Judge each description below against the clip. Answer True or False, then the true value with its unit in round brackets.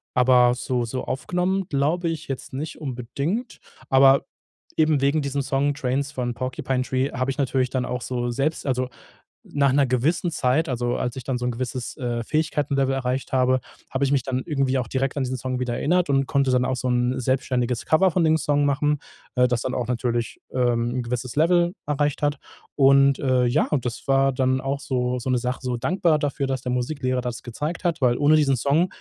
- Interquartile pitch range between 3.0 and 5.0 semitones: False (2.4 semitones)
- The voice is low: True (130 Hz)